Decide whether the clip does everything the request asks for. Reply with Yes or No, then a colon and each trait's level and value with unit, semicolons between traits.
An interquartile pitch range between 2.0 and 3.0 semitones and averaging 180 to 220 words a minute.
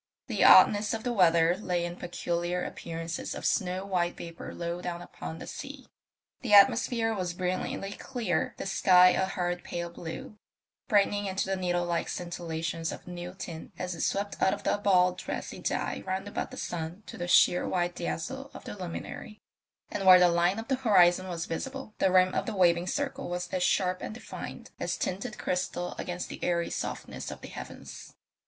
Yes: narrow, 2.4 semitones; average, 190 wpm